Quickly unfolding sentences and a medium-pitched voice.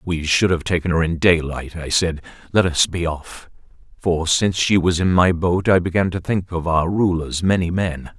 No: fast, 215 wpm; very low, 85 Hz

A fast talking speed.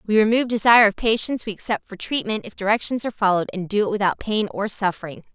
Yes: fast, 225 wpm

